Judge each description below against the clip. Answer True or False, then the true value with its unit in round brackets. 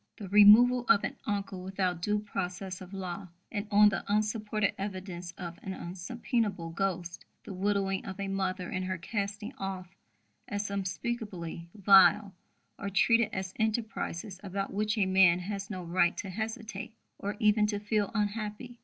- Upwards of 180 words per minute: False (155 wpm)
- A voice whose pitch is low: False (200 Hz)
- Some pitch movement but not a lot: False (2.2 semitones)